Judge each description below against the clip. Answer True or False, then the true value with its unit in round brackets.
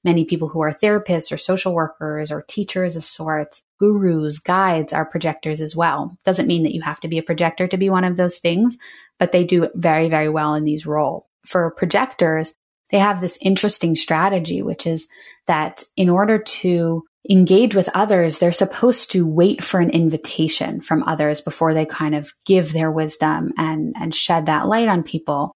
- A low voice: False (170 Hz)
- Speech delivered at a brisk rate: False (190 wpm)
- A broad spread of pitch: False (2.9 semitones)